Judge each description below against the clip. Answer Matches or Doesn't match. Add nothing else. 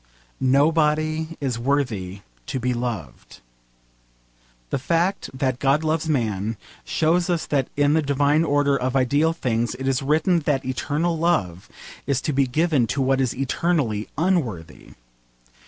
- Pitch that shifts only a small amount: Doesn't match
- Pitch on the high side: Doesn't match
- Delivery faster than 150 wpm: Doesn't match